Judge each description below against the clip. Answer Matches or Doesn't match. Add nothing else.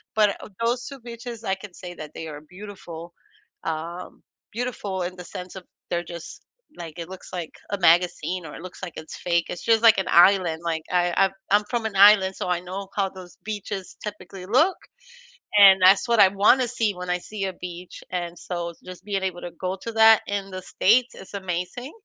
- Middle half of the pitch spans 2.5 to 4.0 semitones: Matches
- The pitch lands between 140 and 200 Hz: Matches